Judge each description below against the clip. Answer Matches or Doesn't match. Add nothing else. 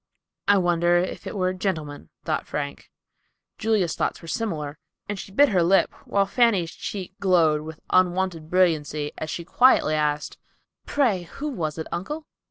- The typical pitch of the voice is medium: Matches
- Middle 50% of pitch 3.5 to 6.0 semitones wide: Matches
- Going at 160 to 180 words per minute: Matches